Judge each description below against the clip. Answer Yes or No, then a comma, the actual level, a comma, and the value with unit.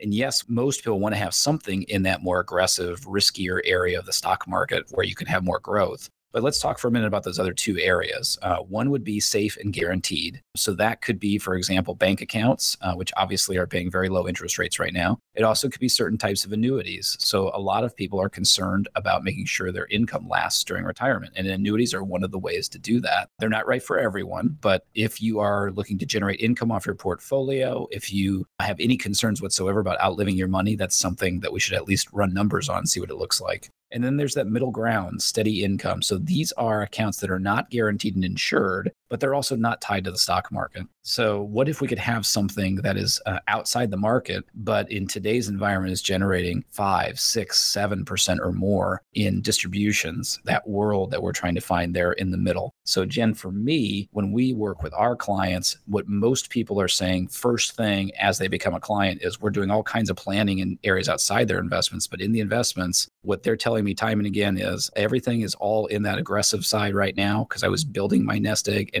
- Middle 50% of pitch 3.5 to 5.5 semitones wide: No, average, 3.0 semitones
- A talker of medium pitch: No, low, 105 Hz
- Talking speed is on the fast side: Yes, fast, 230 wpm